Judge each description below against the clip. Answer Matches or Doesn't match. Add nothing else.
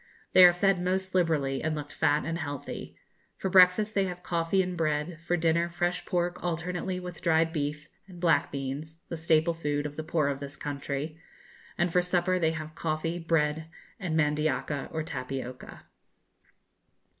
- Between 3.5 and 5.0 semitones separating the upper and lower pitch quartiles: Doesn't match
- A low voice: Doesn't match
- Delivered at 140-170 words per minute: Matches